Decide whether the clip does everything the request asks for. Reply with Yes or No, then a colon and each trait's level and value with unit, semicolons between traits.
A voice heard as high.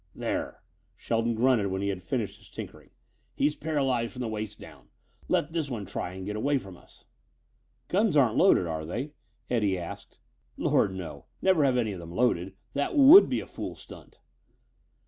No: low, 115 Hz